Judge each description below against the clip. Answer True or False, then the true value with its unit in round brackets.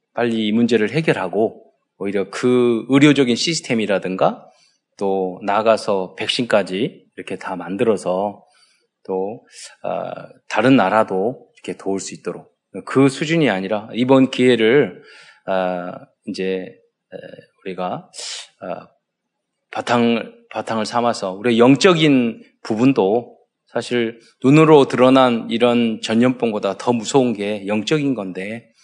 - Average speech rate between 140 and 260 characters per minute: True (240 characters per minute)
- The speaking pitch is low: True (115 Hz)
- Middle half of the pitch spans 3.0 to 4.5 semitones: True (4.0 semitones)